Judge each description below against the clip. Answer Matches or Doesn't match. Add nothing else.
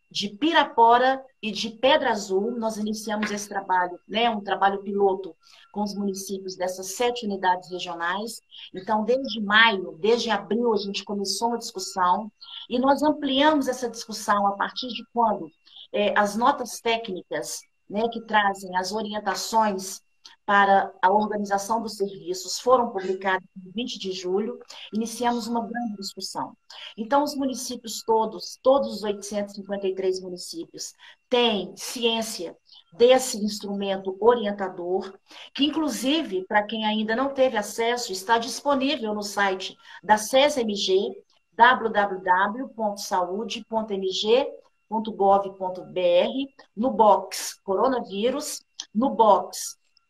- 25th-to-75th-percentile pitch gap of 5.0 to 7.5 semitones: Doesn't match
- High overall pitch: Matches